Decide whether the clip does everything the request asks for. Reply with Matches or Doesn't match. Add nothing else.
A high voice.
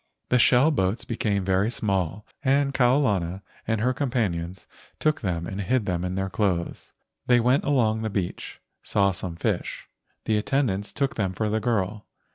Doesn't match